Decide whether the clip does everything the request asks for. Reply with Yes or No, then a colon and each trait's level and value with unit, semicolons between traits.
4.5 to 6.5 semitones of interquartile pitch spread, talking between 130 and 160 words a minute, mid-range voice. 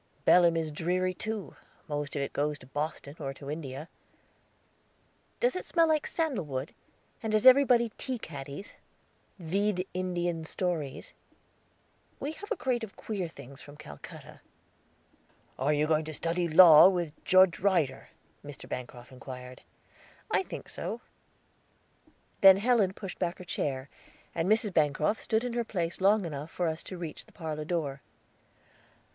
Yes: wide, 5.4 semitones; average, 150 wpm; medium, 170 Hz